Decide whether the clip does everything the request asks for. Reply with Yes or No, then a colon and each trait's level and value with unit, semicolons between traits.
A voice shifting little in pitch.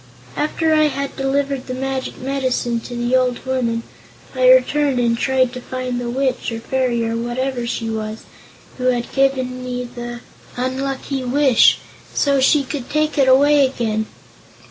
Yes: narrow, 2.1 semitones